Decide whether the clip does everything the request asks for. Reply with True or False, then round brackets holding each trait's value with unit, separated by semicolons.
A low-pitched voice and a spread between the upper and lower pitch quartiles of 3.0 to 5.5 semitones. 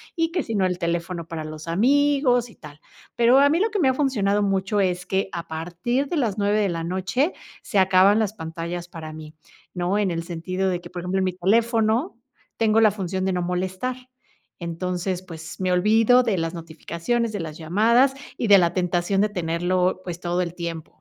False (185 Hz; 4.5 semitones)